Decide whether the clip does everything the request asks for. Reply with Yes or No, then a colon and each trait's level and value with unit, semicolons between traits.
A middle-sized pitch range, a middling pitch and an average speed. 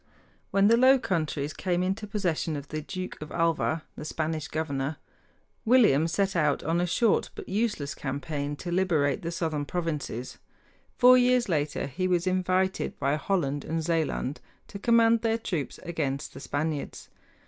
Yes: average, 4.6 semitones; medium, 165 Hz; average, 160 wpm